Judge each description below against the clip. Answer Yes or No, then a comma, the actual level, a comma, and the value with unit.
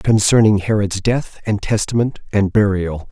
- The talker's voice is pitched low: Yes, low, 105 Hz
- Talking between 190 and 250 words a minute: No, slow, 135 wpm